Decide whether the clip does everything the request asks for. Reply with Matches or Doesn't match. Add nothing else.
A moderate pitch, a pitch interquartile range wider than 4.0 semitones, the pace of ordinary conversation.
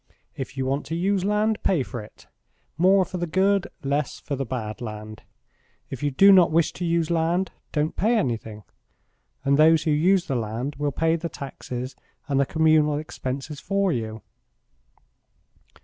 Matches